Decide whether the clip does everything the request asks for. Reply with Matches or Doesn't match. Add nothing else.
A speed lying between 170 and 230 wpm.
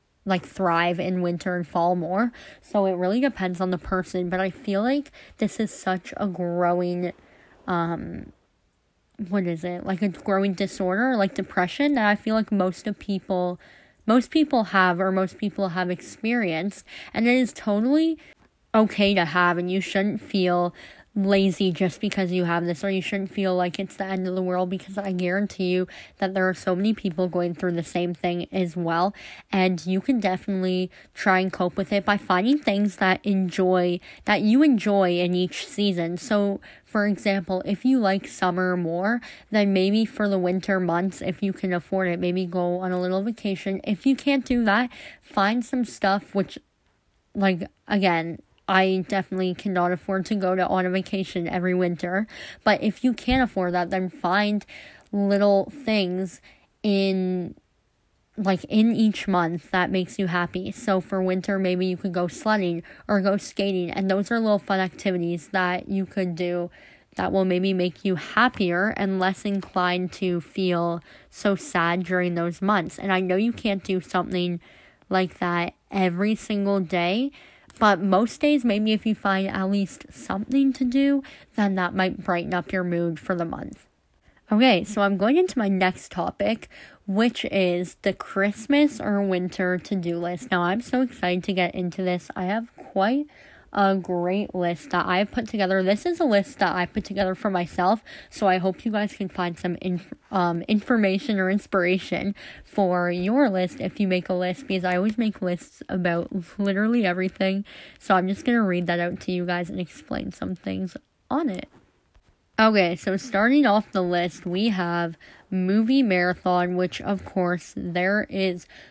Matches